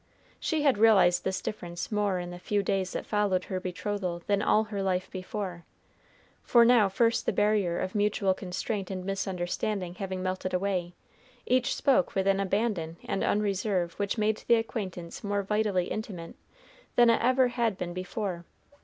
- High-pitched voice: Yes, high, 195 Hz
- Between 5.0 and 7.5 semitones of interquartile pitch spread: No, average, 2.7 semitones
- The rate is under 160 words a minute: No, average, 165 wpm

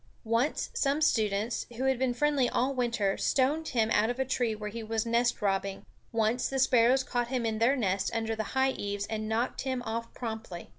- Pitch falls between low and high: No, high, 235 Hz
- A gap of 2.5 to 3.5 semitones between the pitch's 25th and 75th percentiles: Yes, average, 2.9 semitones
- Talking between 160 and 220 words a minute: Yes, average, 200 wpm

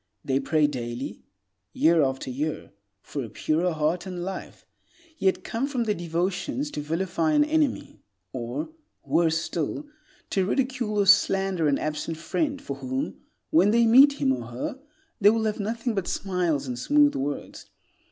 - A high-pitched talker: No, medium, 180 Hz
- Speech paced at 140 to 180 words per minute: Yes, average, 160 wpm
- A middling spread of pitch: No, wide, 7.2 semitones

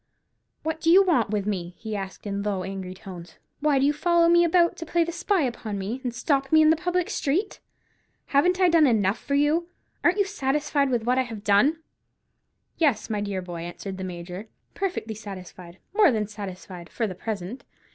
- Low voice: No, high, 240 Hz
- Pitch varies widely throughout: Yes, wide, 8.5 semitones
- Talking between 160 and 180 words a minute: No, average, 195 wpm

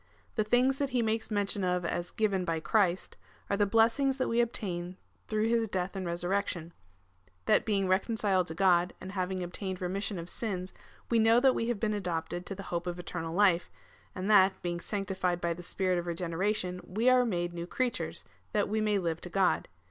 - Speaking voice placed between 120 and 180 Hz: No, high, 190 Hz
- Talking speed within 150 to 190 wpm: No, average, 200 wpm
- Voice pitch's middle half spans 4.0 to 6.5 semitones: No, average, 3.5 semitones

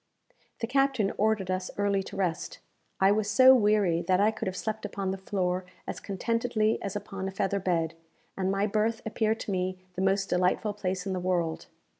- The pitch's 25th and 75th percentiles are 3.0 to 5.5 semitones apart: No, narrow, 2.5 semitones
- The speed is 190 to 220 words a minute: Yes, average, 195 wpm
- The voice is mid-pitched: No, high, 195 Hz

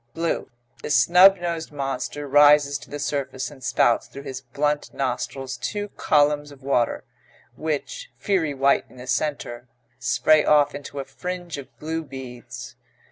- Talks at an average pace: Yes, average, 150 wpm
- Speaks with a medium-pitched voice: Yes, medium, 145 Hz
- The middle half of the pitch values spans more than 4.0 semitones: No, narrow, 2.5 semitones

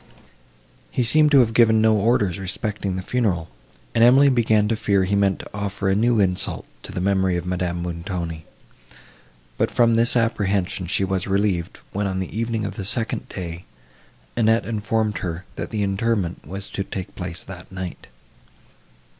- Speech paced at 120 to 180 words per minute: Yes, average, 170 wpm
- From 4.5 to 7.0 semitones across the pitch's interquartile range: No, average, 3.4 semitones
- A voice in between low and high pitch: No, low, 100 Hz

